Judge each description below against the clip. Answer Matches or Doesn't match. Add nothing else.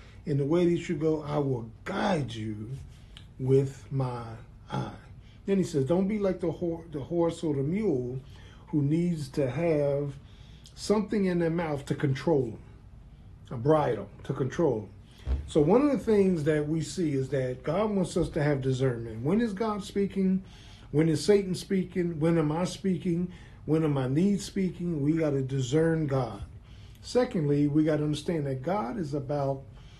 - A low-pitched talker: Doesn't match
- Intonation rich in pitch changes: Doesn't match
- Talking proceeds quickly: Doesn't match